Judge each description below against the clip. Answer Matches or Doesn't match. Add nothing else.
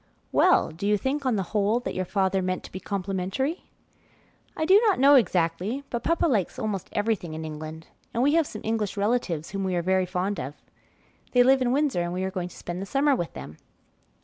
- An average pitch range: Doesn't match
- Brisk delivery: Matches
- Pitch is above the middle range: Matches